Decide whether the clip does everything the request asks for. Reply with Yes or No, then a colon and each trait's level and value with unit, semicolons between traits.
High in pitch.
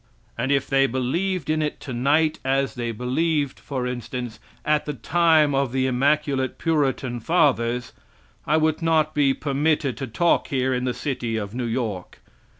No: low, 135 Hz